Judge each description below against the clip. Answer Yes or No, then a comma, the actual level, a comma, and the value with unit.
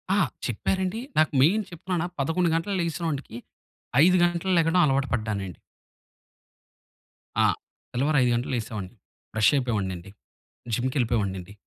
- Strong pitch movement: Yes, wide, 7.7 semitones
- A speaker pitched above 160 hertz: No, low, 135 Hz